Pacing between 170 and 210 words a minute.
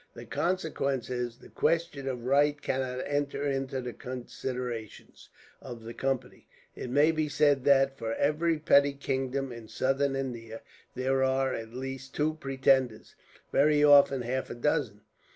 No: average, 150 wpm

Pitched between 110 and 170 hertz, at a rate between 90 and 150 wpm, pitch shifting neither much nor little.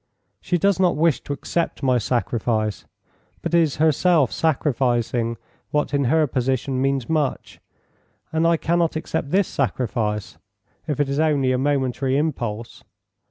Yes: medium, 140 Hz; average, 140 wpm; average, 4.3 semitones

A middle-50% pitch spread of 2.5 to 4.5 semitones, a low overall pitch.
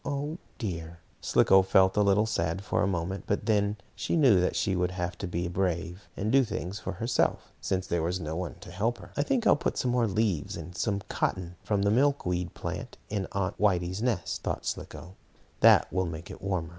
Yes: average, 3.4 semitones; very low, 95 Hz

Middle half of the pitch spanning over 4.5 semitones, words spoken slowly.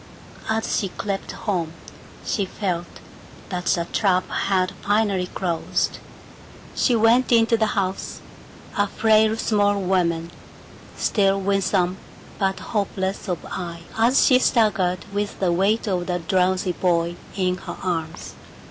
No: average, 2.7 semitones; slow, 130 wpm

